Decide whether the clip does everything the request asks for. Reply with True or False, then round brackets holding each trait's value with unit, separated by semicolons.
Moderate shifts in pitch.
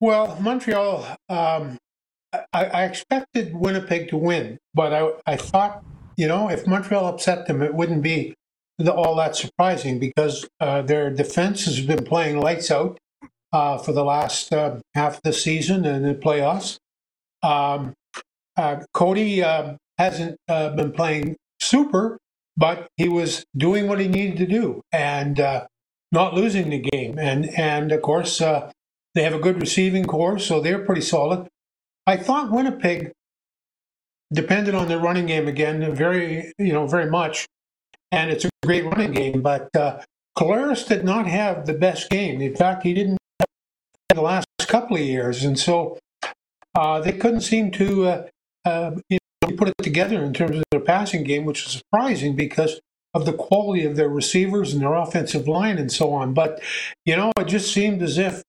True (3.9 semitones)